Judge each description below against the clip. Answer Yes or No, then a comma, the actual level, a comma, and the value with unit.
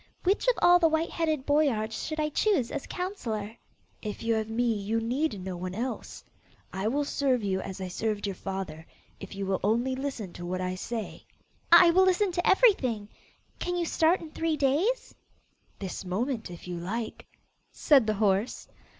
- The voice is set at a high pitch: Yes, high, 235 Hz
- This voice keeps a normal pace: Yes, average, 185 wpm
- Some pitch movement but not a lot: No, wide, 7.8 semitones